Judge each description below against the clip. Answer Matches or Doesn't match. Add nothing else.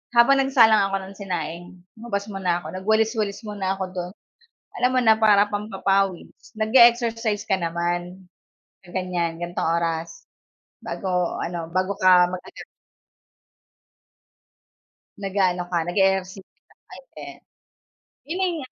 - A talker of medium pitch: Doesn't match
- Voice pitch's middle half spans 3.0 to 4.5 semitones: Matches